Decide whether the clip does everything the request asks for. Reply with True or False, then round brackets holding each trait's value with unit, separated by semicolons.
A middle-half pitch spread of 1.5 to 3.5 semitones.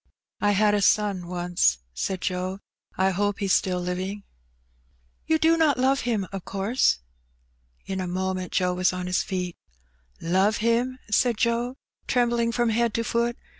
False (4.3 semitones)